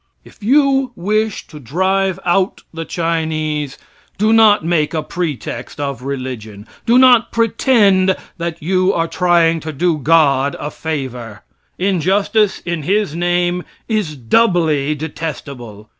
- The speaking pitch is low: No, medium, 170 Hz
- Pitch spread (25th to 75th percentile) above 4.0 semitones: Yes, average, 4.8 semitones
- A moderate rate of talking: No, slow, 130 wpm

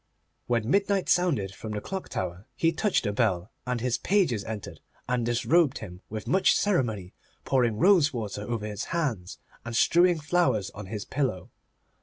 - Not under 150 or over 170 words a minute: Yes, average, 165 wpm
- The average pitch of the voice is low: Yes, low, 120 Hz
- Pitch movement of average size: No, wide, 8.2 semitones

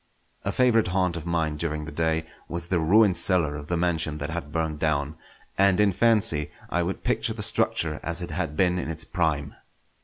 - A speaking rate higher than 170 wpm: Yes, fast, 205 wpm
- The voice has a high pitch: No, very low, 85 Hz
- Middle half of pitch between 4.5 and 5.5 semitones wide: No, average, 2.8 semitones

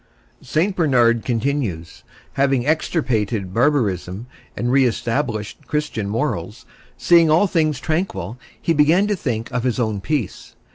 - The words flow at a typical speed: No, slow, 130 wpm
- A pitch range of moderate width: No, wide, 5.7 semitones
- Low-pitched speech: Yes, low, 130 Hz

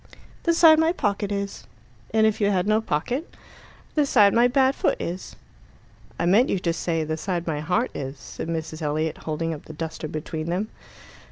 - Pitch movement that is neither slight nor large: No, wide, 5.7 semitones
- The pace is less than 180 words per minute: No, average, 190 wpm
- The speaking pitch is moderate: Yes, medium, 180 Hz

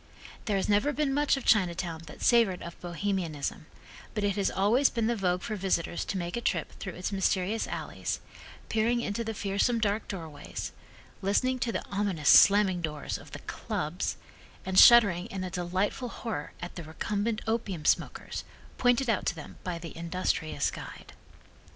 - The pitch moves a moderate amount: Yes, average, 4.3 semitones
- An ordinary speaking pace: Yes, average, 170 wpm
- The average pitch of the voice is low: No, high, 195 Hz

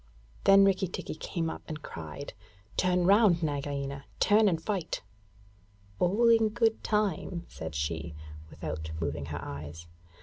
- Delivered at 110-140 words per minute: Yes, slow, 135 wpm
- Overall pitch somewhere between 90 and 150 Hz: No, medium, 165 Hz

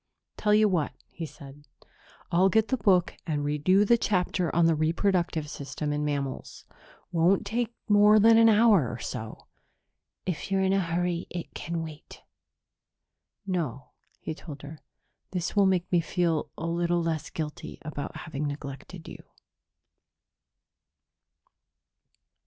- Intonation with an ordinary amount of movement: Yes, average, 4.3 semitones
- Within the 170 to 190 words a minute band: No, average, 140 wpm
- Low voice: No, medium, 170 Hz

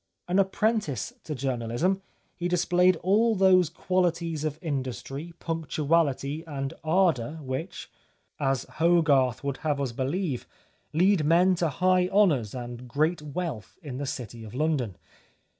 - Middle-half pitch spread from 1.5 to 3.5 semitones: No, average, 4.9 semitones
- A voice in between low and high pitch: Yes, medium, 155 Hz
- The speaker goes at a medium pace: No, slow, 130 wpm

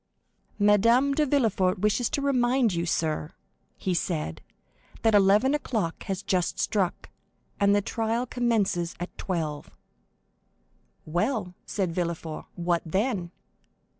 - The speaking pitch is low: No, high, 200 Hz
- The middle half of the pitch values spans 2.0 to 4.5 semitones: No, average, 5.2 semitones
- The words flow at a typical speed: No, slow, 120 wpm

